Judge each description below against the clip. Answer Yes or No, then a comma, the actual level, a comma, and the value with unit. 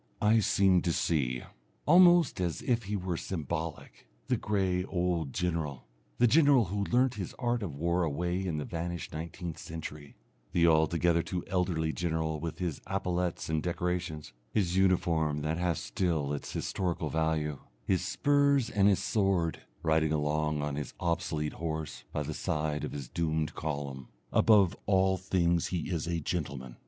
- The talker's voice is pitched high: No, very low, 85 Hz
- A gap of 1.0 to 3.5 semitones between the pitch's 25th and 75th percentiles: Yes, average, 3.2 semitones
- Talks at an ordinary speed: Yes, average, 160 wpm